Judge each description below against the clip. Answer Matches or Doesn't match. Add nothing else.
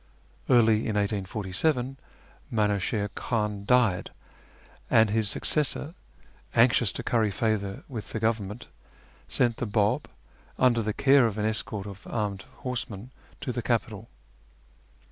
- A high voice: Doesn't match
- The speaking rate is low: Matches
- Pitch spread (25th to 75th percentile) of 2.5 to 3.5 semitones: Matches